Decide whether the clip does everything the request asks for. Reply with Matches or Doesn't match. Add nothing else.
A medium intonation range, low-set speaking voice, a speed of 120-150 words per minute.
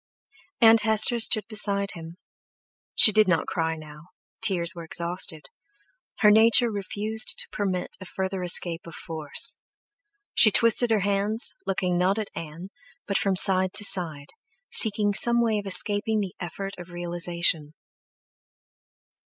Doesn't match